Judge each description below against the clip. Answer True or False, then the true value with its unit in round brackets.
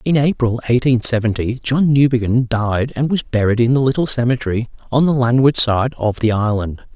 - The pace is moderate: True (180 wpm)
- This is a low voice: True (120 Hz)